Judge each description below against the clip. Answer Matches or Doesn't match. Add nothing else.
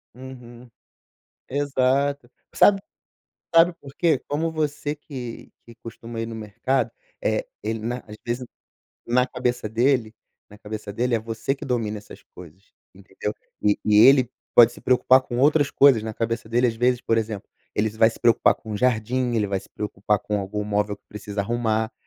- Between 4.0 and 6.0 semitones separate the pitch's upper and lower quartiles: Doesn't match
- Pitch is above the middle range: Doesn't match